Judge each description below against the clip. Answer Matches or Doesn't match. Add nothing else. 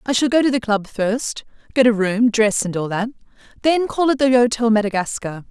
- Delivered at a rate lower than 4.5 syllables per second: Doesn't match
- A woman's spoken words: Matches